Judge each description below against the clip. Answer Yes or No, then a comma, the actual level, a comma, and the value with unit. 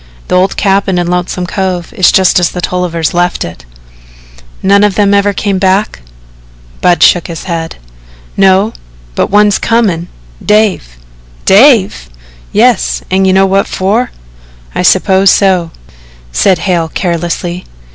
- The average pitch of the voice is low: No, medium, 185 Hz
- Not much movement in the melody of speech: Yes, narrow, 2.2 semitones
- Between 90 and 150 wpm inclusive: Yes, slow, 135 wpm